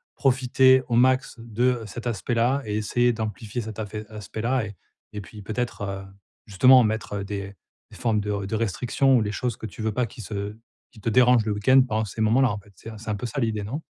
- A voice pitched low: Yes, low, 110 Hz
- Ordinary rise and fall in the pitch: Yes, average, 3.0 semitones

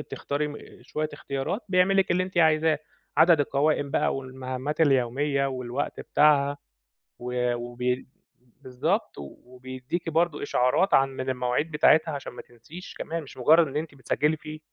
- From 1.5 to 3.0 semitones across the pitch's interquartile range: No, average, 3.7 semitones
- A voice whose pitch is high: No, medium, 140 Hz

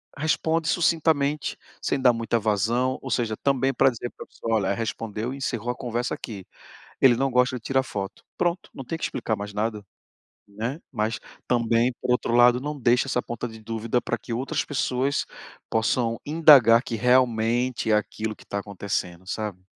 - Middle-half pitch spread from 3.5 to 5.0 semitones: No, average, 3.1 semitones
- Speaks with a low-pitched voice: Yes, low, 120 Hz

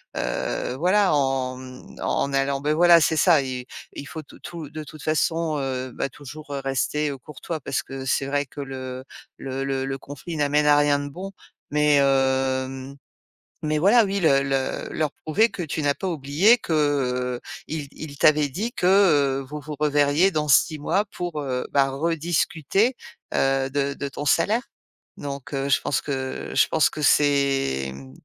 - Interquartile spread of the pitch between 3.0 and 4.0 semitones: No, narrow, 2.6 semitones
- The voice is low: No, medium, 145 Hz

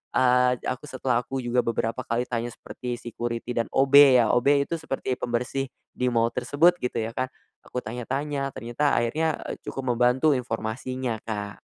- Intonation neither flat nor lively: No, narrow, 2.0 semitones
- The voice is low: Yes, low, 125 Hz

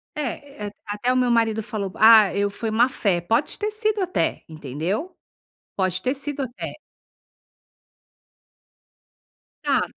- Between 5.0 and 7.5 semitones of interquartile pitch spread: Yes, wide, 5.5 semitones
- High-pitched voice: Yes, high, 225 Hz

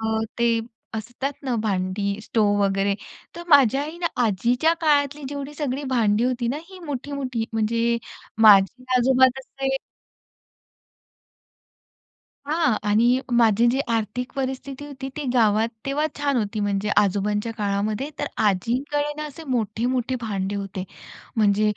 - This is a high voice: Yes, high, 235 Hz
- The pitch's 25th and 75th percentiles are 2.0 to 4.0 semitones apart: No, average, 4.7 semitones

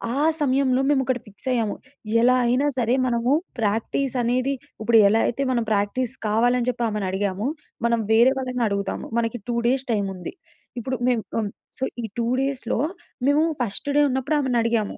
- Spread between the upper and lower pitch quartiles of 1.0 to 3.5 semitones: Yes, average, 2.8 semitones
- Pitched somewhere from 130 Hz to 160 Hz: No, high, 240 Hz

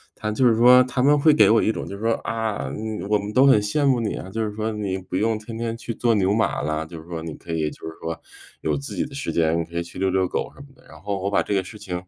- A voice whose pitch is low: Yes, low, 105 Hz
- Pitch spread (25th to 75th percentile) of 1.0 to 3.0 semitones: No, average, 4.2 semitones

